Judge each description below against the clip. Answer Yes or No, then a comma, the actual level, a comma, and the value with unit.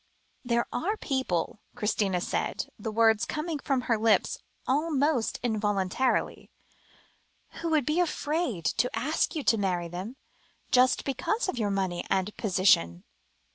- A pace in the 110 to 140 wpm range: Yes, slow, 135 wpm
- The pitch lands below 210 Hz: No, high, 230 Hz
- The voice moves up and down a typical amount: No, wide, 6.7 semitones